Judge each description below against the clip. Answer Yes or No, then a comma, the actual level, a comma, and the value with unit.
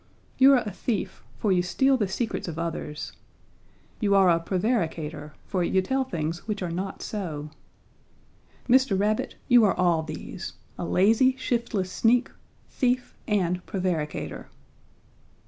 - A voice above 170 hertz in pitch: Yes, high, 190 Hz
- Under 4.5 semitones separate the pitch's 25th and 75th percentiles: No, wide, 5.6 semitones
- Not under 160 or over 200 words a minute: No, average, 140 wpm